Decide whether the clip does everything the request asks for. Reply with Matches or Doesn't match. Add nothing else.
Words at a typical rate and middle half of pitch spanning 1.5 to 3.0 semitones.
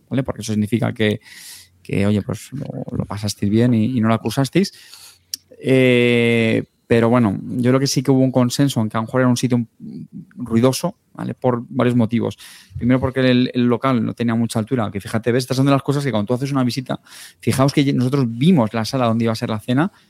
Doesn't match